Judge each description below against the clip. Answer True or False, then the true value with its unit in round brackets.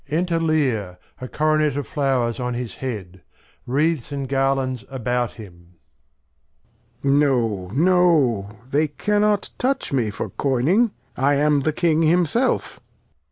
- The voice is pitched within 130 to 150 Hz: True (135 Hz)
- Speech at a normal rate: False (125 wpm)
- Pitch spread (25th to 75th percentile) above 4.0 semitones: True (4.5 semitones)